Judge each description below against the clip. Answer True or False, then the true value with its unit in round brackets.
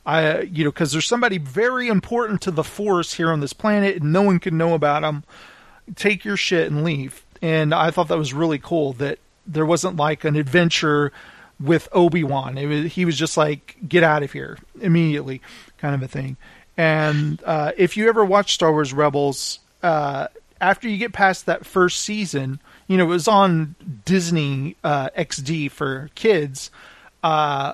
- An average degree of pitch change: True (3.8 semitones)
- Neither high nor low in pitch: True (160 Hz)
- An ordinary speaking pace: True (185 wpm)